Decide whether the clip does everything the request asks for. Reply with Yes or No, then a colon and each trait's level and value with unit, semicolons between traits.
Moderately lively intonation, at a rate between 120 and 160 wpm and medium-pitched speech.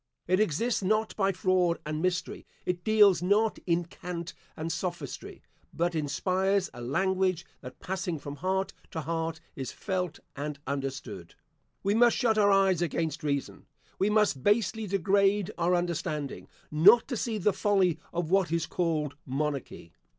Yes: average, 3.9 semitones; average, 150 wpm; medium, 180 Hz